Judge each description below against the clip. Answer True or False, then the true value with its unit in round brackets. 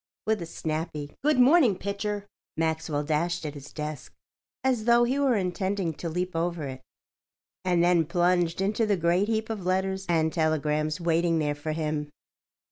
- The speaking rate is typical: True (165 wpm)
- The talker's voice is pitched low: False (175 Hz)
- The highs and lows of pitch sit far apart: False (4.2 semitones)